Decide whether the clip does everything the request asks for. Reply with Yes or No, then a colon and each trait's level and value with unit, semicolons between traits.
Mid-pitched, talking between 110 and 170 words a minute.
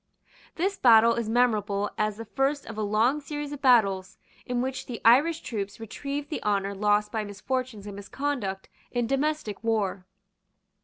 No: high, 225 Hz; average, 160 wpm